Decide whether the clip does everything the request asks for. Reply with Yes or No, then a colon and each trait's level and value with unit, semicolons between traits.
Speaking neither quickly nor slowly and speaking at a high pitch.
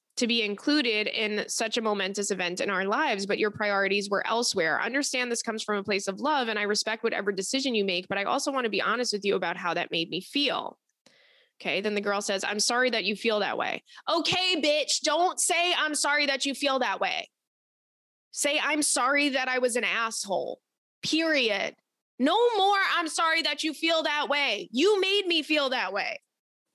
No: fast, 210 wpm; high, 245 Hz